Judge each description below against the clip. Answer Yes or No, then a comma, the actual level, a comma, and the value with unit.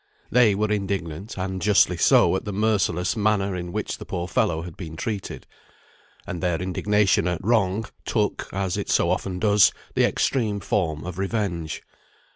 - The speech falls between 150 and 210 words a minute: Yes, average, 165 wpm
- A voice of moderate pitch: No, very low, 95 Hz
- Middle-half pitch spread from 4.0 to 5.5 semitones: No, average, 2.9 semitones